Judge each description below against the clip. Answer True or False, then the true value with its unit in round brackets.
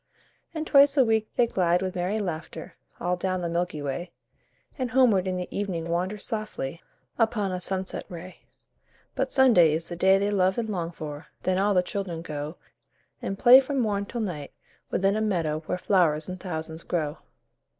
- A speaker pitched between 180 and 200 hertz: True (185 Hz)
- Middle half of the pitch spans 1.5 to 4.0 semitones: True (3.7 semitones)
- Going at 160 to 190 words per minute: True (180 wpm)